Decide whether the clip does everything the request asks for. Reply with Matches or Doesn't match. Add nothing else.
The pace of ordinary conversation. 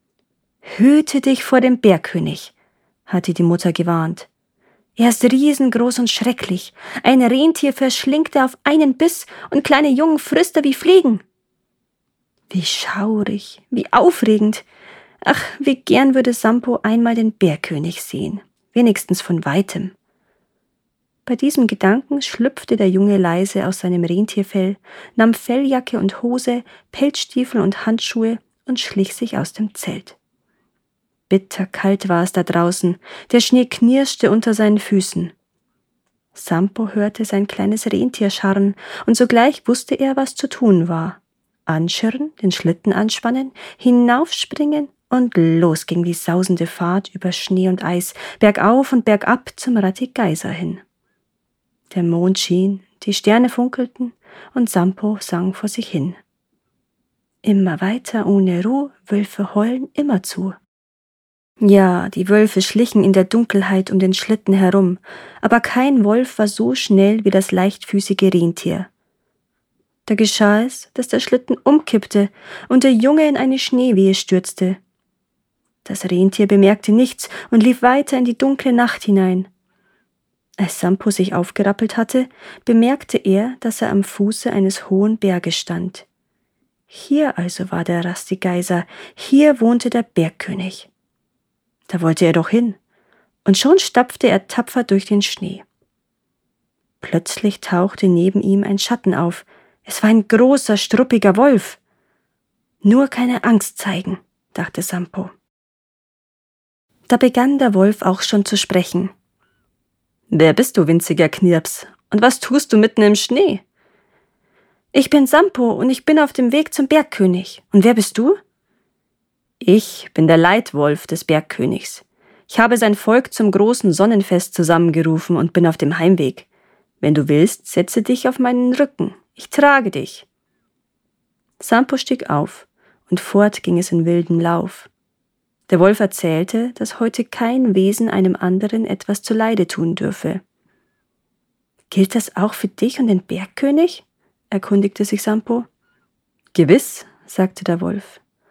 Matches